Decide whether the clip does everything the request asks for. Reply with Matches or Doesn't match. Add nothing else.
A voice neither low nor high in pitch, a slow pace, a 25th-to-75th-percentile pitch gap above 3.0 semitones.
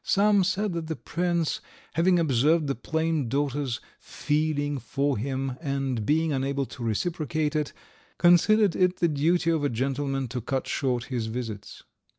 Doesn't match